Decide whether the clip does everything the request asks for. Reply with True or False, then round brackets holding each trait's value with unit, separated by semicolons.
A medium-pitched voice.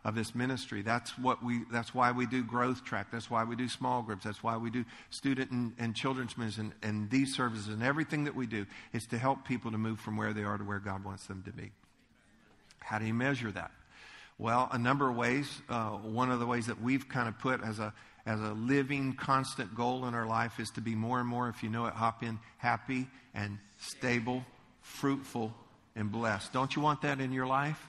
False (120 Hz)